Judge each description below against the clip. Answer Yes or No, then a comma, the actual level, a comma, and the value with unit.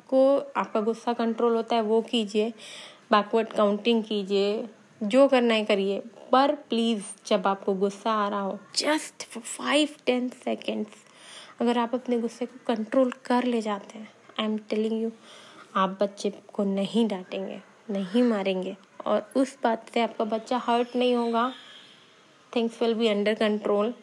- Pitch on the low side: No, high, 225 Hz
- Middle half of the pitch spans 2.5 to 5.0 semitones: Yes, average, 2.8 semitones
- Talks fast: No, average, 155 wpm